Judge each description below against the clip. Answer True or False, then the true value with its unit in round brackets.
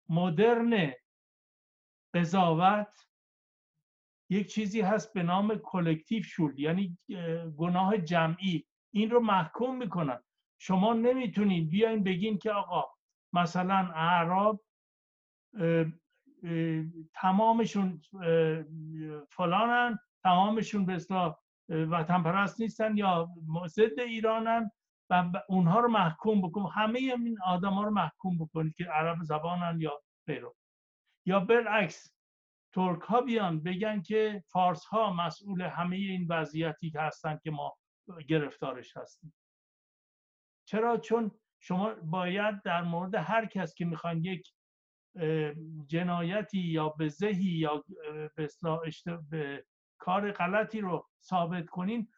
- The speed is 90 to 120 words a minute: True (110 wpm)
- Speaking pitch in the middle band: True (180 Hz)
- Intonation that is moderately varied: True (4.5 semitones)